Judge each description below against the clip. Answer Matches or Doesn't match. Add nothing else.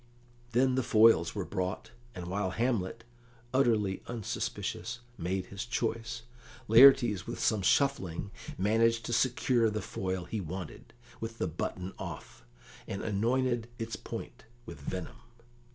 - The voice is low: Matches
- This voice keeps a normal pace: Doesn't match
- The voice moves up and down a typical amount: Matches